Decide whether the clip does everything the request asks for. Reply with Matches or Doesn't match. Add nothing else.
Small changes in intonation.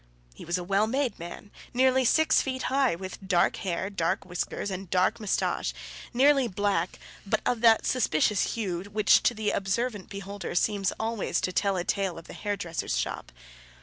Doesn't match